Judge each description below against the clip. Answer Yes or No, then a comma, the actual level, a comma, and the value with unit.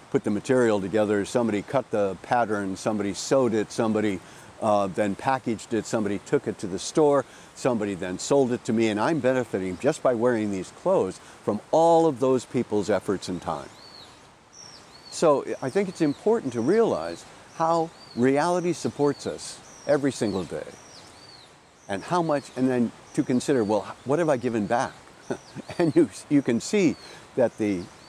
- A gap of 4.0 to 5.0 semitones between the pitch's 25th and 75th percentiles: No, wide, 5.6 semitones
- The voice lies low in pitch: Yes, low, 125 Hz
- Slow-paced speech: No, average, 165 wpm